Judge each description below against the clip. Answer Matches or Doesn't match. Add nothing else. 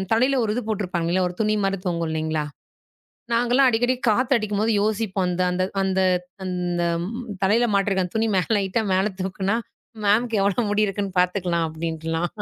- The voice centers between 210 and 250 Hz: Doesn't match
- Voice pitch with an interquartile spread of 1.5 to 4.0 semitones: Matches